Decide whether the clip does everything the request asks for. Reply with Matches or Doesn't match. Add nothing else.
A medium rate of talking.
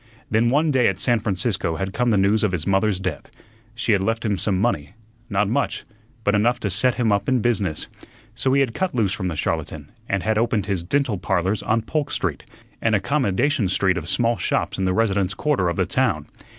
Doesn't match